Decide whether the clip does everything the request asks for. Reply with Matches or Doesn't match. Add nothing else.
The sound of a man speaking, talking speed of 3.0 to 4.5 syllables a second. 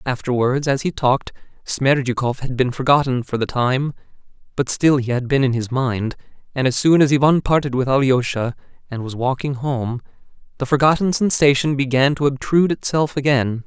Doesn't match